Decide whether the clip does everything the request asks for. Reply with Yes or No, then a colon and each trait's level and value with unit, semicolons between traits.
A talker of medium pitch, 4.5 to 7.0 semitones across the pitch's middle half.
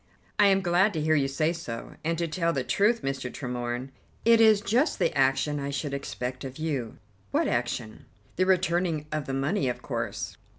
Yes: medium, 150 Hz; average, 5.3 semitones